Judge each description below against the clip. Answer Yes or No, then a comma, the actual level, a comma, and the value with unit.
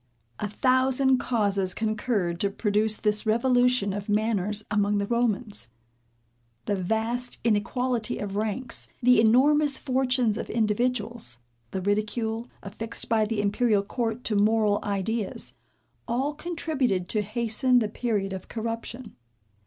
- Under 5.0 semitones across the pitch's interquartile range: Yes, average, 3.2 semitones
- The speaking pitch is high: Yes, high, 220 Hz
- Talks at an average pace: No, slow, 125 wpm